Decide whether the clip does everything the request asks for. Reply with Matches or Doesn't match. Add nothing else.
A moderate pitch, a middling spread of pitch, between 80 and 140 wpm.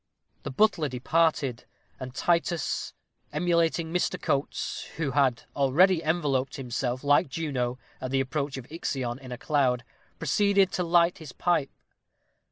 Matches